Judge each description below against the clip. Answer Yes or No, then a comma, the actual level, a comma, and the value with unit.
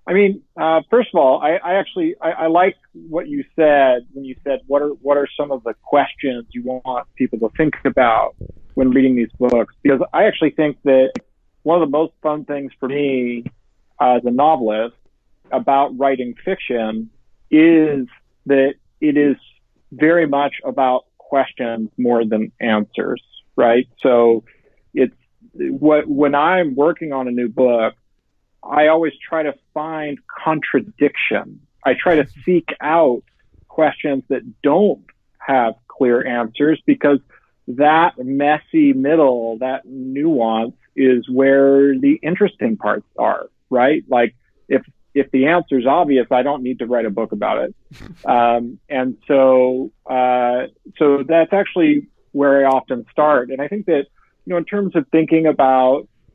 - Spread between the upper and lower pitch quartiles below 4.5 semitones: Yes, average, 4.0 semitones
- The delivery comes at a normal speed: Yes, average, 155 wpm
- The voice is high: No, medium, 140 Hz